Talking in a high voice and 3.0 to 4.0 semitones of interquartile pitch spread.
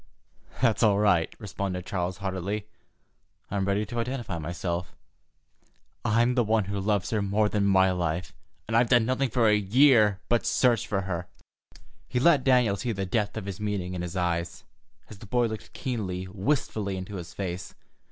No: low, 100 Hz; average, 3.6 semitones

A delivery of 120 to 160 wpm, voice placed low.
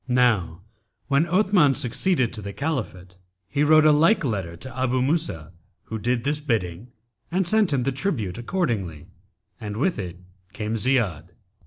Yes: average, 155 wpm; low, 125 Hz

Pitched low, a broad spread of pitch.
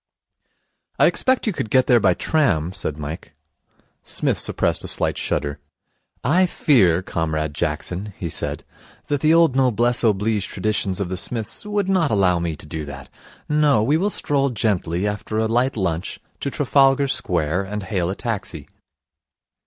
Yes: low, 105 Hz; wide, 7.6 semitones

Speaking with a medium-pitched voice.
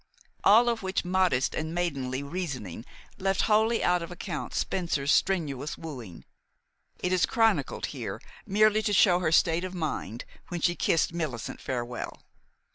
Yes: medium, 175 Hz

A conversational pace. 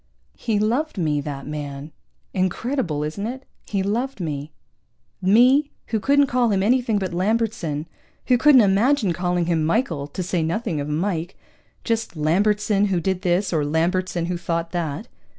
Yes: average, 155 wpm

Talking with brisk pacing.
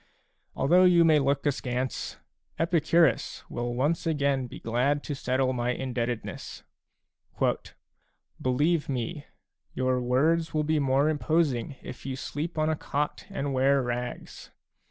No: slow, 135 wpm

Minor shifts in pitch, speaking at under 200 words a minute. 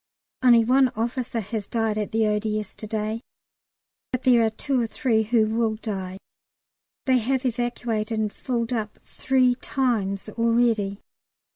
Yes: narrow, 2.3 semitones; average, 145 wpm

